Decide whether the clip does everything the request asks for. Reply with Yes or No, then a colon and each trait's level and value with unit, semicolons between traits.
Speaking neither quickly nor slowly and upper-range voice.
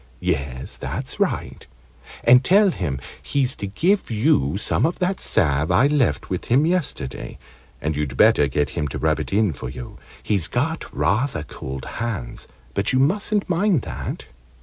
No: average, 165 wpm; low, 105 Hz